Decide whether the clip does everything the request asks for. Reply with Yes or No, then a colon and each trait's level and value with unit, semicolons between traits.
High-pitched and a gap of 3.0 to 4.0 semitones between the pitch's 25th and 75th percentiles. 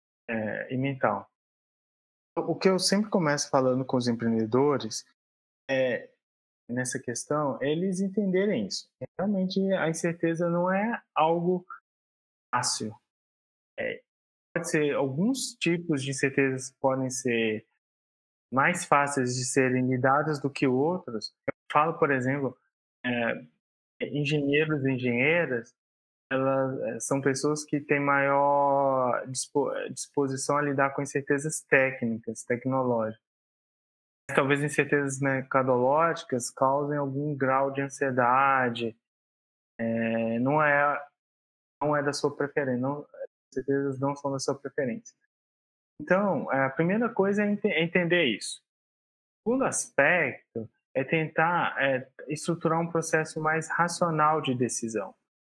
No: medium, 140 Hz; average, 3.7 semitones